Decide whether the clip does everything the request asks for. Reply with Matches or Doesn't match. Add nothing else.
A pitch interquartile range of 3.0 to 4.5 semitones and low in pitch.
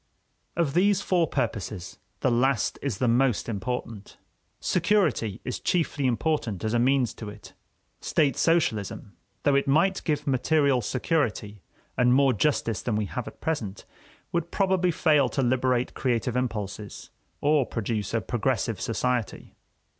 Doesn't match